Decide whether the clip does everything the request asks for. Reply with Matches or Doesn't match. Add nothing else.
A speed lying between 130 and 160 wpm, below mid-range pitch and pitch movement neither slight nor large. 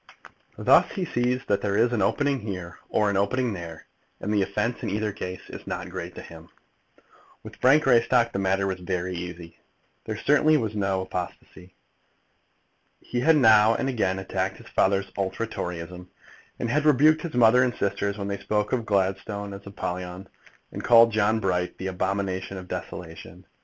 Doesn't match